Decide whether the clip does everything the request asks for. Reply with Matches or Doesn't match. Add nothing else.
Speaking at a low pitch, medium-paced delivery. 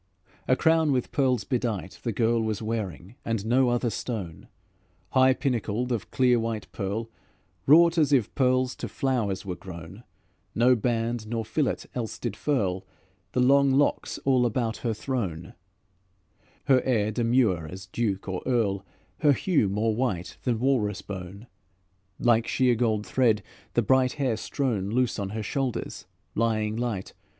Matches